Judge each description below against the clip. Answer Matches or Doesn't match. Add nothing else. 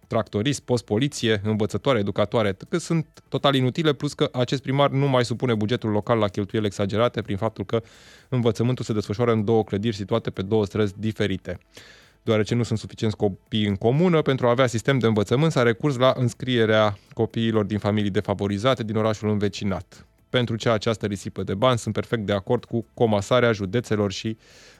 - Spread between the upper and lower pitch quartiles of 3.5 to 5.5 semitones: Doesn't match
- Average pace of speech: Doesn't match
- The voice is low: Matches